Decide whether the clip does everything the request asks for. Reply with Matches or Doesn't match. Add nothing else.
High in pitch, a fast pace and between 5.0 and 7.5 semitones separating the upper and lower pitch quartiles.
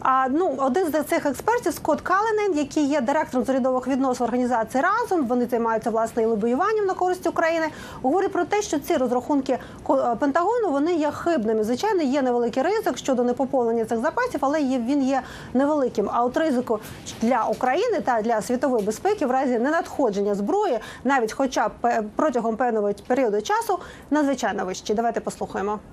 Matches